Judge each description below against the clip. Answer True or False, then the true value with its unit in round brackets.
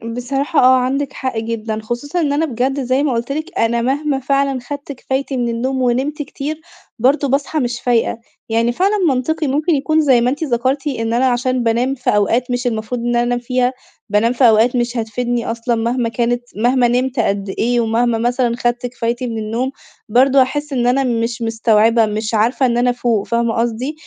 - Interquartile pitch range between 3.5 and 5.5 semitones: False (2.5 semitones)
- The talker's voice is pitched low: False (245 Hz)